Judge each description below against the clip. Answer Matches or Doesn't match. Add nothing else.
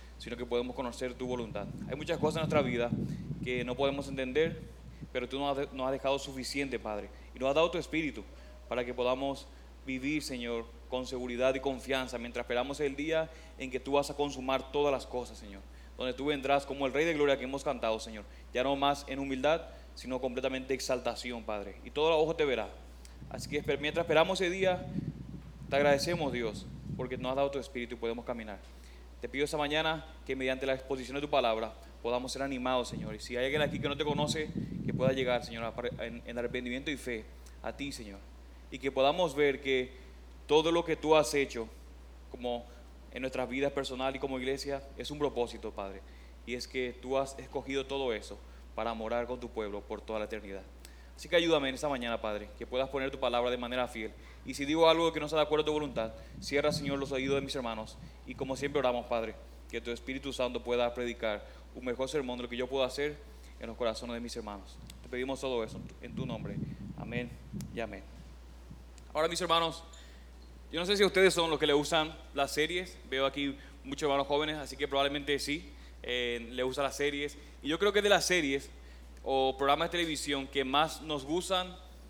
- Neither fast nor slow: Doesn't match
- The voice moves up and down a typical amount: Matches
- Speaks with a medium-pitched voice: Doesn't match